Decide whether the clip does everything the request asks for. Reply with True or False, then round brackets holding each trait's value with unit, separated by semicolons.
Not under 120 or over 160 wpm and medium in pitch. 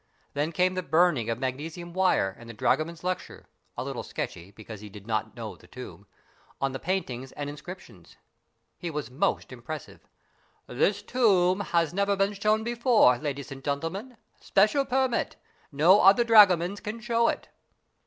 True (155 wpm; 175 Hz)